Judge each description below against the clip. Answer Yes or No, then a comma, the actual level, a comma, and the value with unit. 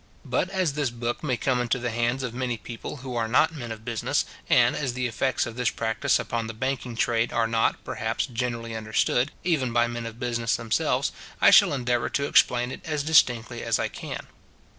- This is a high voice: No, low, 120 Hz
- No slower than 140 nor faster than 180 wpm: No, fast, 205 wpm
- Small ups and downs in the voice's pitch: Yes, narrow, 2.0 semitones